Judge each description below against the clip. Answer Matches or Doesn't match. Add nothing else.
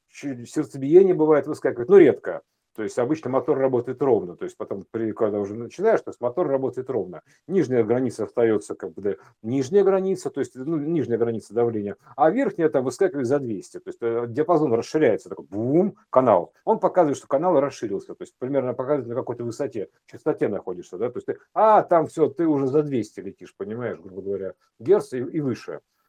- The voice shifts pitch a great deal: Matches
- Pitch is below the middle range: Doesn't match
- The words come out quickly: Matches